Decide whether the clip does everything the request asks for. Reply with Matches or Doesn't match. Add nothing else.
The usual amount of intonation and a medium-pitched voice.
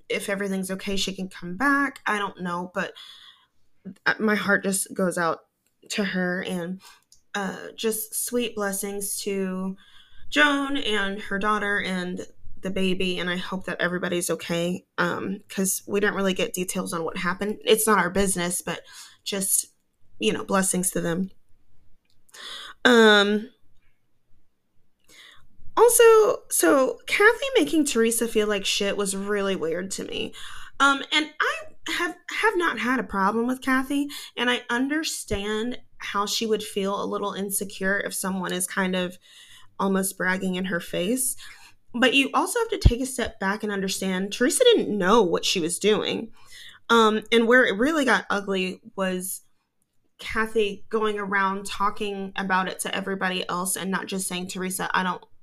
Doesn't match